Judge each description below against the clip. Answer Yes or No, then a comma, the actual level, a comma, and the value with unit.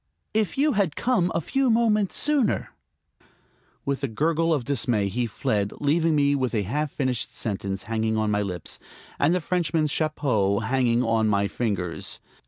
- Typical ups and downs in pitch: No, wide, 7.4 semitones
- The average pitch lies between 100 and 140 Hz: Yes, low, 135 Hz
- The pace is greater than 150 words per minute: Yes, average, 165 wpm